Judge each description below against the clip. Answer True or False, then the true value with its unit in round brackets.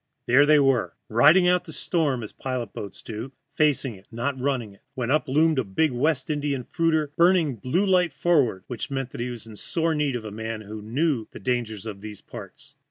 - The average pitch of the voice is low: True (130 Hz)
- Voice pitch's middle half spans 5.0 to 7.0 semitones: True (5.3 semitones)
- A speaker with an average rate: False (225 wpm)